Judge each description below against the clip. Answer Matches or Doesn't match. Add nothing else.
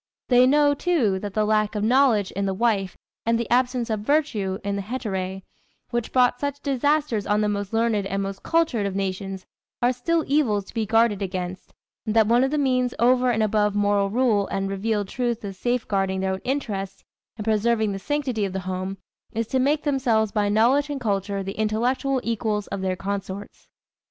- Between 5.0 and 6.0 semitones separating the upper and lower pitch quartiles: Doesn't match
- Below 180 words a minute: Doesn't match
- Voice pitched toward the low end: Doesn't match